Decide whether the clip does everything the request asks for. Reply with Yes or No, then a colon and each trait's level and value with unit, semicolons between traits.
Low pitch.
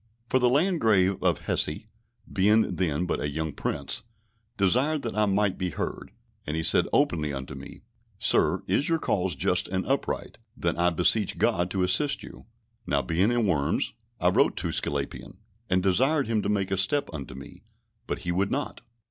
Yes: very low, 95 Hz